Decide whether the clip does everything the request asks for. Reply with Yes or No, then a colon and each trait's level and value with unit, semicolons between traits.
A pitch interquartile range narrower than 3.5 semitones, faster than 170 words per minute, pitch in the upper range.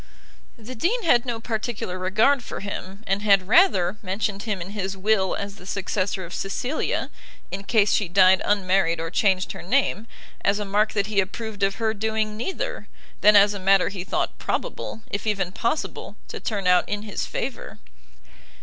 Yes: narrow, 2.5 semitones; average, 180 wpm; high, 200 Hz